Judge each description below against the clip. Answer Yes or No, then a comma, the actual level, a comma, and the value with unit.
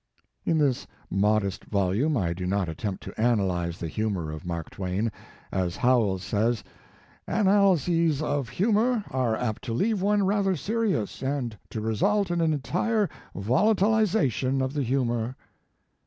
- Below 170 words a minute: Yes, average, 150 wpm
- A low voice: Yes, low, 125 Hz